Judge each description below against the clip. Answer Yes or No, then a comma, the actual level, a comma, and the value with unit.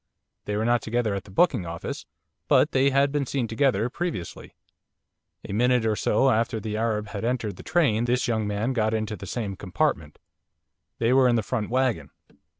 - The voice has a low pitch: Yes, low, 115 Hz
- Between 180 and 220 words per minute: Yes, average, 190 wpm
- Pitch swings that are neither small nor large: Yes, average, 3.3 semitones